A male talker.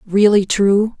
No: female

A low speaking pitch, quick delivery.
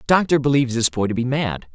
Yes: low, 130 Hz; fast, 275 wpm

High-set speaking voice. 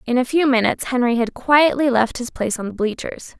Yes: high, 245 Hz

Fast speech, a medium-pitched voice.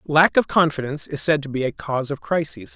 Yes: fast, 240 wpm; medium, 145 Hz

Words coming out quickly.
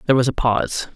Yes: fast, 250 wpm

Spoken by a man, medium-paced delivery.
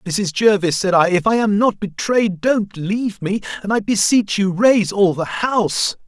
Yes: male; average, 195 wpm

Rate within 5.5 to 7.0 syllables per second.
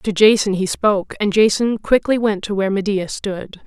No: 5.0 syllables/s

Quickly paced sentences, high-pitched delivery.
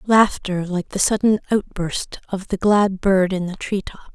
No: average, 190 wpm; high, 195 Hz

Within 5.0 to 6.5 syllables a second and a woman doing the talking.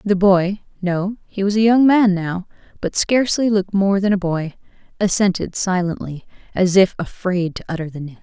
Yes: 5.1 syllables/s; female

